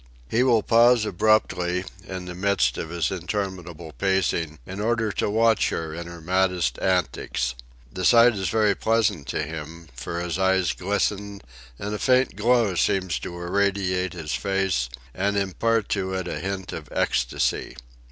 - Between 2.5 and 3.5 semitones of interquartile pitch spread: Yes, average, 3.1 semitones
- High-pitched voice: No, very low, 95 Hz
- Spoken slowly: No, average, 160 wpm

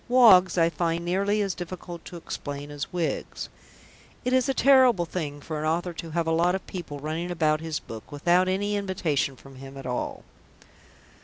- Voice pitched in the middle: Yes, medium, 170 Hz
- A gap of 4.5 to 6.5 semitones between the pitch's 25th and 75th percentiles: No, average, 3.4 semitones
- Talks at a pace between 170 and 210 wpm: Yes, average, 185 wpm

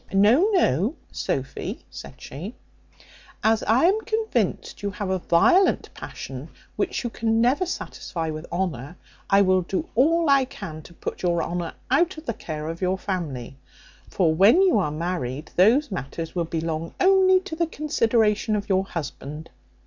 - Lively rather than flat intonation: Yes, wide, 8.2 semitones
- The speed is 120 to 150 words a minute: No, average, 165 wpm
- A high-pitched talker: Yes, high, 195 Hz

